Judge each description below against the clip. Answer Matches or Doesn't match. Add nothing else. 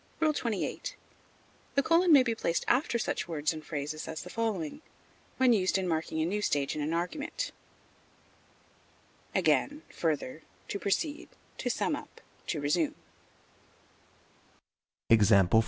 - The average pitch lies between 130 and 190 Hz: Matches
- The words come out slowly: Matches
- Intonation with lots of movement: Matches